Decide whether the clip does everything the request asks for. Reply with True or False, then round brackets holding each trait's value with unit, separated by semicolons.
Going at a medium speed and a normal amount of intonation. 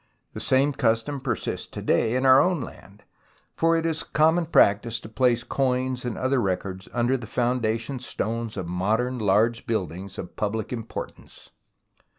True (170 wpm; 3.1 semitones)